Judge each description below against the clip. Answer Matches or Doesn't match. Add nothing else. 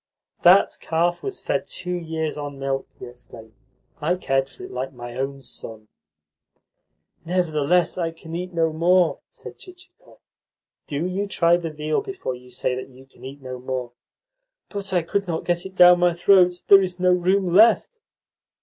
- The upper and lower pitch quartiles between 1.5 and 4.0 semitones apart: Doesn't match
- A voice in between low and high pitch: Matches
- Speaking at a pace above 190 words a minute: Doesn't match